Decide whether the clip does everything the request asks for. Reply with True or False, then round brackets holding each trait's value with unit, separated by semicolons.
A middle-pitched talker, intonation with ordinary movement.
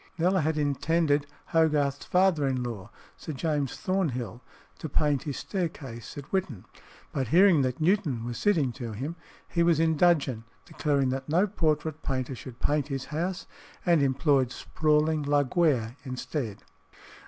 True (145 Hz; 3.9 semitones)